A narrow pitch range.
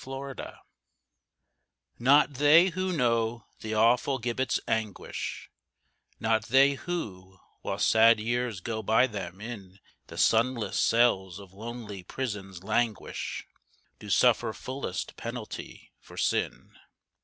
No: average, 3.9 semitones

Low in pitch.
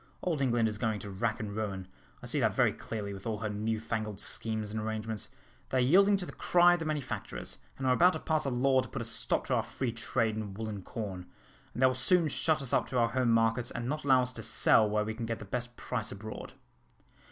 Yes: low, 115 Hz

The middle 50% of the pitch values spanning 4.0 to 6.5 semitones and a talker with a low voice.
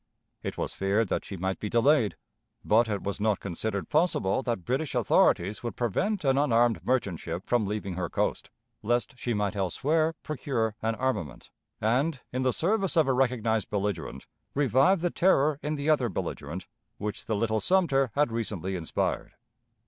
Yes: wide, 5.4 semitones; low, 115 Hz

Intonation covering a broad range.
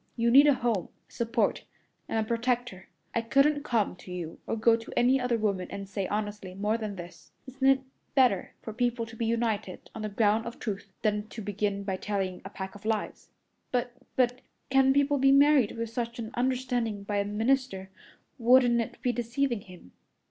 No: average, 3.4 semitones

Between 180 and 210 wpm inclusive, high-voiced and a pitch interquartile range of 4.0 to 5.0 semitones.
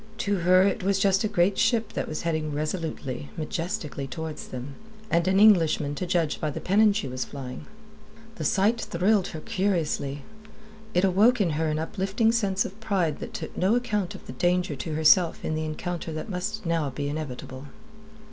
No: average, 185 wpm; medium, 175 Hz; average, 4.5 semitones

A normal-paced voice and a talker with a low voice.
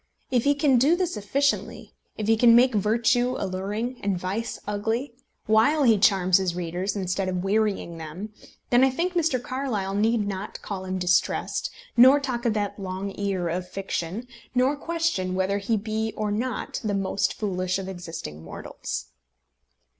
No: average, 165 wpm; high, 210 Hz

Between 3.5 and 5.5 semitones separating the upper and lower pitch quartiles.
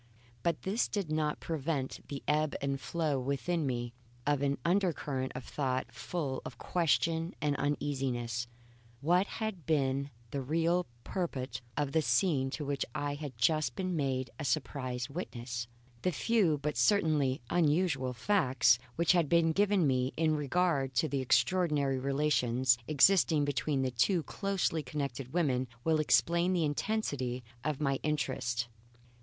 Yes: average, 4.1 semitones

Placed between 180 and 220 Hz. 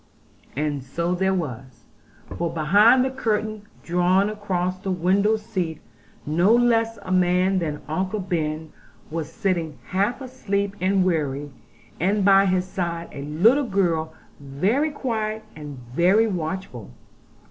Yes: medium, 185 Hz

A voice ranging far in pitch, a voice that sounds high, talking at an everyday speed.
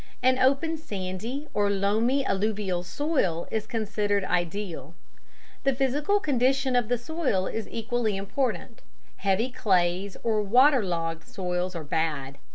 No: wide, 5.7 semitones; high, 210 Hz; slow, 130 wpm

